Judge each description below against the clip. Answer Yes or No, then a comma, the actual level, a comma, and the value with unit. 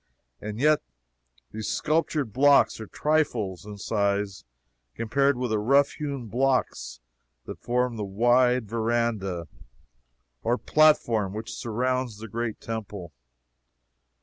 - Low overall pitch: Yes, low, 115 Hz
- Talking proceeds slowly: Yes, slow, 115 wpm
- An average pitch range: Yes, average, 3.7 semitones